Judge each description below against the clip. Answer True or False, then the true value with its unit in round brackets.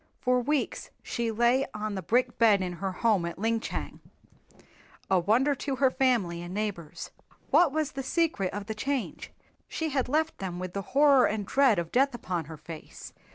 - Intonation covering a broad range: True (6.1 semitones)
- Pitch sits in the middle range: False (225 Hz)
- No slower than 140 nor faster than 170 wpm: False (185 wpm)